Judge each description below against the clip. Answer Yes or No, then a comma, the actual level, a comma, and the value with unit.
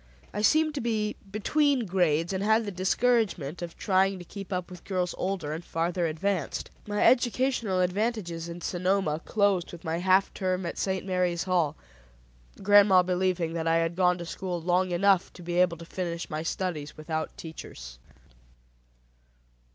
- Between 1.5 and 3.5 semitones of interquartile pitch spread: Yes, average, 2.8 semitones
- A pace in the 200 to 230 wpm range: No, average, 165 wpm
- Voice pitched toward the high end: No, medium, 180 Hz